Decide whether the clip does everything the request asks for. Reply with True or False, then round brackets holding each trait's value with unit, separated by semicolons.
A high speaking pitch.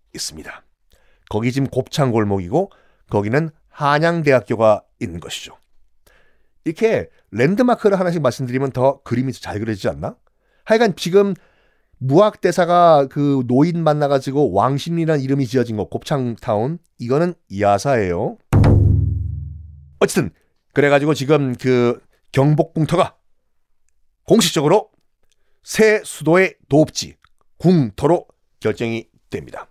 False (140 Hz)